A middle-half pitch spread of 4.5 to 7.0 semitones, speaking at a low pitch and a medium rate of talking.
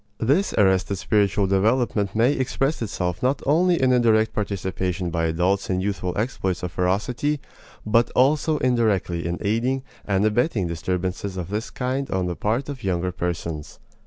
Yes: wide, 5.5 semitones; low, 105 Hz; average, 160 wpm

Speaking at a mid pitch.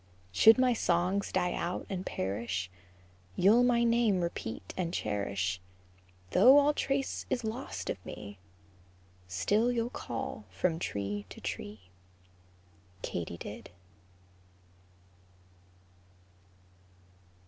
Yes: medium, 175 Hz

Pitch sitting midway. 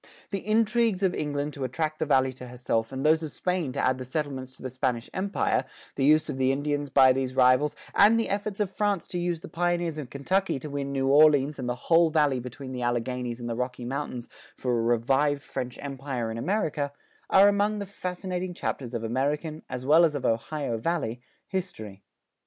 Yes: medium, 145 Hz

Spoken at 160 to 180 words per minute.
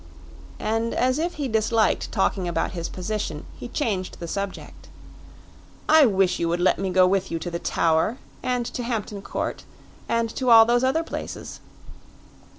Yes: average, 165 wpm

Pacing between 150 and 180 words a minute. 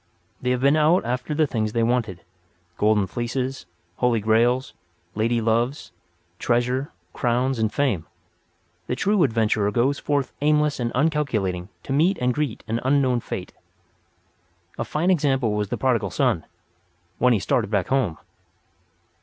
No: slow, 135 wpm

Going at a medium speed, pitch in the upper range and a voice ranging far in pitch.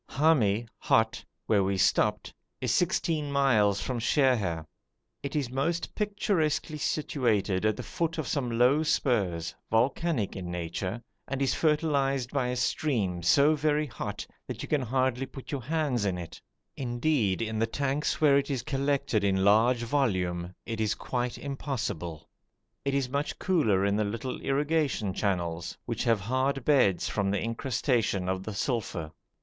No: average, 155 wpm; low, 125 Hz; wide, 5.7 semitones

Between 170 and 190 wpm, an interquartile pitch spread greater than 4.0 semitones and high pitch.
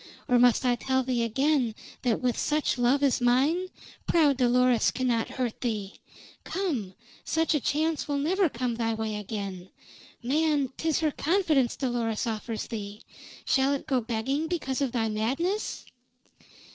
No: average, 150 wpm; average, 4.4 semitones; very high, 255 Hz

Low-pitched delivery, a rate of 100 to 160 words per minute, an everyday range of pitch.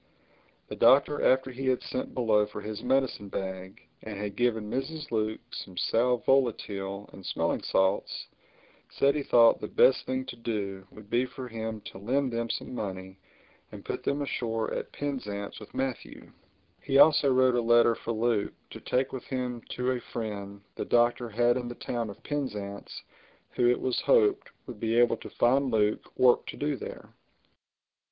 No: low, 120 Hz; average, 175 wpm; average, 3.7 semitones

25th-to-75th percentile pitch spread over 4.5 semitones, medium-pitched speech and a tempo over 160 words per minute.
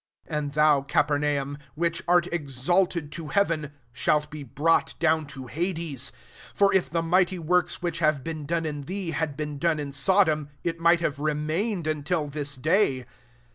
No: average, 2.8 semitones; medium, 155 Hz; average, 170 wpm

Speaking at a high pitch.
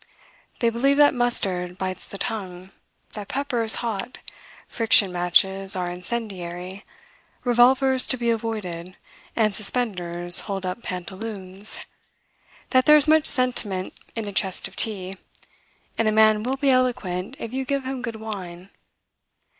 Yes: high, 215 Hz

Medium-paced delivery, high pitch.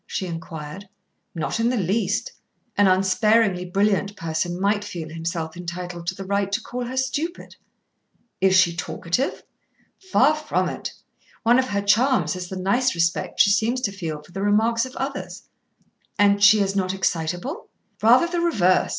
Yes: average, 165 wpm; high, 200 Hz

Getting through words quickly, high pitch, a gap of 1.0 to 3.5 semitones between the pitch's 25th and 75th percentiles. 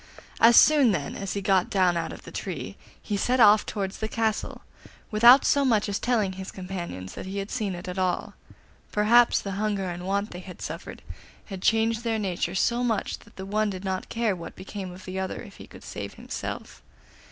Yes: fast, 210 wpm; high, 200 Hz; average, 3.0 semitones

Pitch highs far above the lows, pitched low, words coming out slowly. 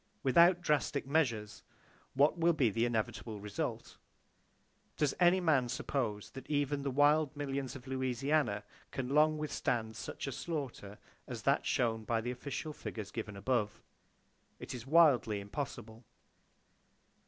No: average, 4.7 semitones; low, 130 Hz; slow, 130 wpm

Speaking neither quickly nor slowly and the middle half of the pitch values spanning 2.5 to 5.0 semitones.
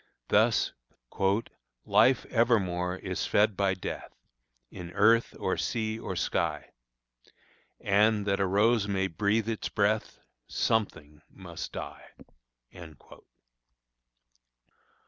No: slow, 95 wpm; average, 2.8 semitones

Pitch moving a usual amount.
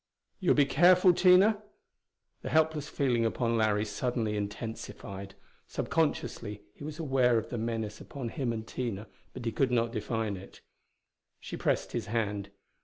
Yes: average, 4.8 semitones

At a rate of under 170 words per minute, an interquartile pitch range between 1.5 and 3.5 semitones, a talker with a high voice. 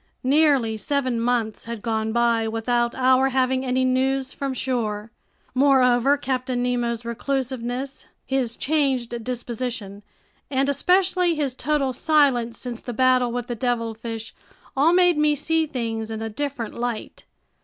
Yes: slow, 135 wpm; average, 2.7 semitones; very high, 250 Hz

